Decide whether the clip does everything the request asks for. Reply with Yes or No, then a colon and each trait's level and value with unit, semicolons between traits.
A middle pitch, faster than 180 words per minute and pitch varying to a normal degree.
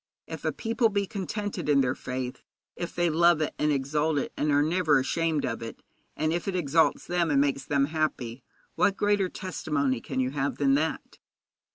Yes: medium, 155 Hz; average, 195 wpm; average, 4.1 semitones